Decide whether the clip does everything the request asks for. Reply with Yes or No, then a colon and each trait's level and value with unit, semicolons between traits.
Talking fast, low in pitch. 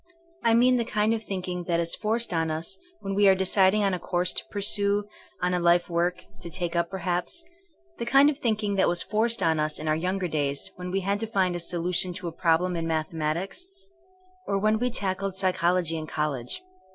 No: fast, 235 wpm; medium, 185 Hz